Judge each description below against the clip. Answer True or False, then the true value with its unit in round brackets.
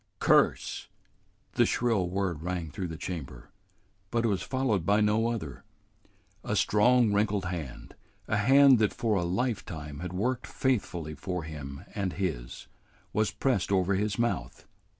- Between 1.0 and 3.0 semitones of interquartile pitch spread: False (4.9 semitones)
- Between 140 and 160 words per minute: True (150 wpm)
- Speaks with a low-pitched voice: True (100 Hz)